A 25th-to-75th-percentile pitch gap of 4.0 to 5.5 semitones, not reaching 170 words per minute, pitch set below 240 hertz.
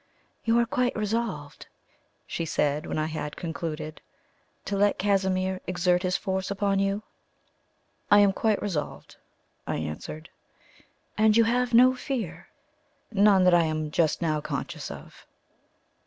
Yes: average, 4.8 semitones; average, 140 wpm; high, 190 Hz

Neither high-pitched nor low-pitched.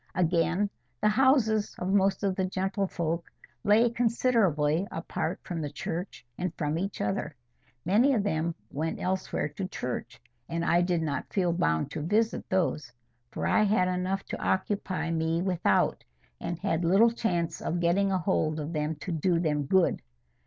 Yes: medium, 180 Hz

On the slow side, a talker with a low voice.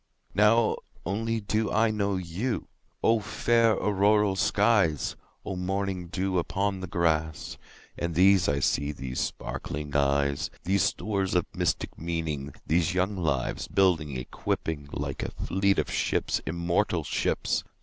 Yes: slow, 110 wpm; very low, 90 Hz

